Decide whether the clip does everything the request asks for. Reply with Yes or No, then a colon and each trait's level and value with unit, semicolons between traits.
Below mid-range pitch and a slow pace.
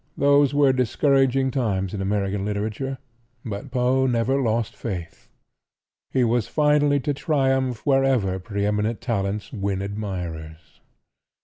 Yes: low, 115 Hz; slow, 120 wpm